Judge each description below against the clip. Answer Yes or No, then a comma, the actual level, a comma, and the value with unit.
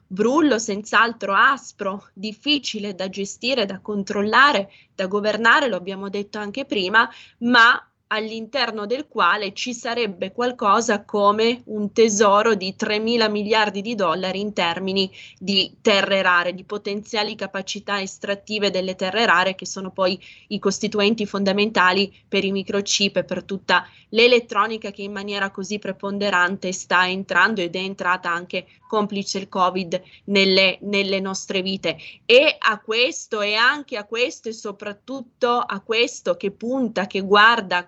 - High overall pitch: Yes, high, 205 Hz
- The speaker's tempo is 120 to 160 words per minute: Yes, average, 140 wpm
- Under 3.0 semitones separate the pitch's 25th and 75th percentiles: Yes, narrow, 2.5 semitones